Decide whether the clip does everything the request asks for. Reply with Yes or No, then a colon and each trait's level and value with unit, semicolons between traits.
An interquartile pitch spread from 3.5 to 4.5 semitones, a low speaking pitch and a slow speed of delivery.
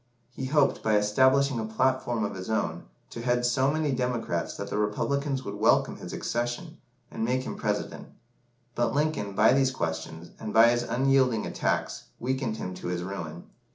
No: average, 4.1 semitones; low, 120 Hz; average, 175 wpm